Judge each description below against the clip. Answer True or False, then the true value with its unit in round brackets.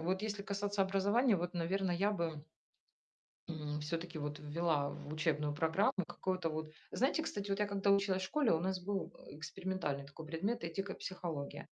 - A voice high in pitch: False (180 Hz)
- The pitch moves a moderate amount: True (4.0 semitones)